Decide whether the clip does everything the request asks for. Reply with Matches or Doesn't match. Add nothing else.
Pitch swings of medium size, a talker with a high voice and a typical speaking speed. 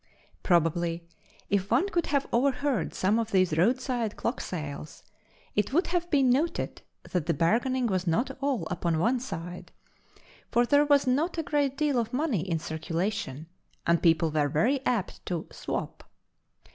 Doesn't match